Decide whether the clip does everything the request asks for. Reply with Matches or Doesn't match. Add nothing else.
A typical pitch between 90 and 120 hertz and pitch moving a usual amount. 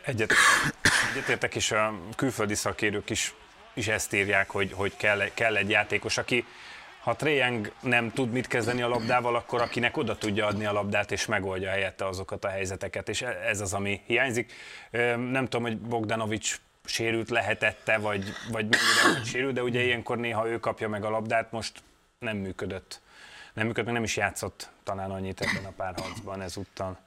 Matches